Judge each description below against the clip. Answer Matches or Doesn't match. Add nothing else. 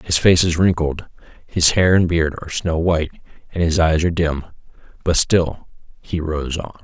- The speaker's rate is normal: Matches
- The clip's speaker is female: Doesn't match